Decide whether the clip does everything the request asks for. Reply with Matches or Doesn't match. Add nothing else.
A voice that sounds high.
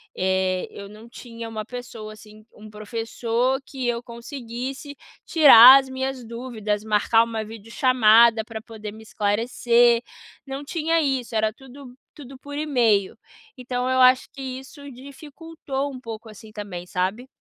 Matches